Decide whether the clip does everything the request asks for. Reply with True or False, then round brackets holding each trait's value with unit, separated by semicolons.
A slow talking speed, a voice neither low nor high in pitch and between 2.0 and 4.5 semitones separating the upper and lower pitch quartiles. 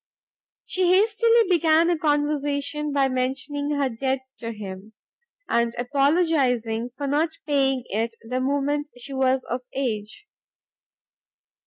False (120 wpm; 275 Hz; 3.4 semitones)